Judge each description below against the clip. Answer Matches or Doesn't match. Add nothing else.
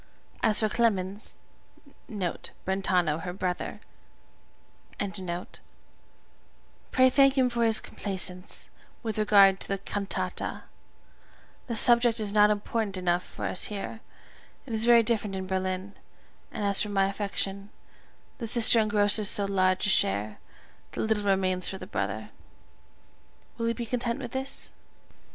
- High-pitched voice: Matches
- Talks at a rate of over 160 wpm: Doesn't match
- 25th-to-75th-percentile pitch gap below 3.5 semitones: Matches